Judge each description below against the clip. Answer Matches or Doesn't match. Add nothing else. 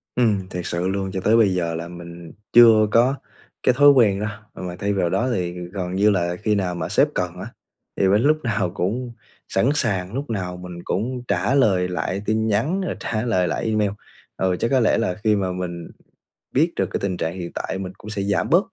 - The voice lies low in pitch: Matches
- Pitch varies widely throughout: Doesn't match